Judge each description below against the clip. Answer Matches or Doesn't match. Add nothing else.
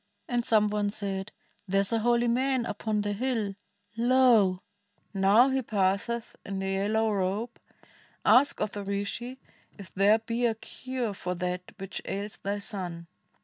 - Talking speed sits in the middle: Matches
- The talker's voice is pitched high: Matches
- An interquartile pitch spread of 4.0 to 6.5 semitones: Doesn't match